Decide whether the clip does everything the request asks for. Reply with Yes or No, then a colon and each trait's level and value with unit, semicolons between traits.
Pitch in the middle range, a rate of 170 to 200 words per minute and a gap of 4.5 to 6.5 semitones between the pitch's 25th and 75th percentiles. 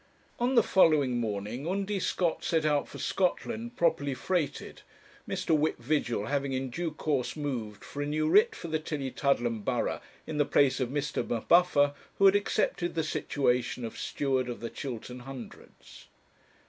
No: medium, 145 Hz; average, 160 wpm; average, 4.8 semitones